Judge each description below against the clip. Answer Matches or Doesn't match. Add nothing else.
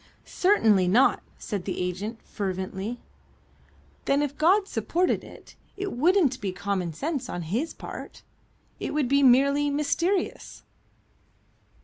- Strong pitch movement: Matches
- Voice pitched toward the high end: Matches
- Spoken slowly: Matches